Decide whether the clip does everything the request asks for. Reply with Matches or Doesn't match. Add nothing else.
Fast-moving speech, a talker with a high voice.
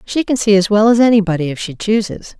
Matches